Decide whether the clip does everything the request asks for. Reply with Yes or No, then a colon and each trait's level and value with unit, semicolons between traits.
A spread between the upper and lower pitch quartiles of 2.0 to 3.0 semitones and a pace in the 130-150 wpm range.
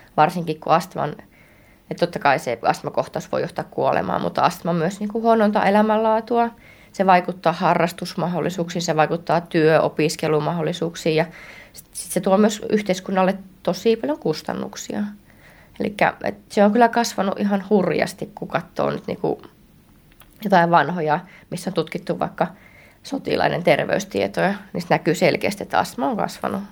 No: average, 4.0 semitones; average, 135 wpm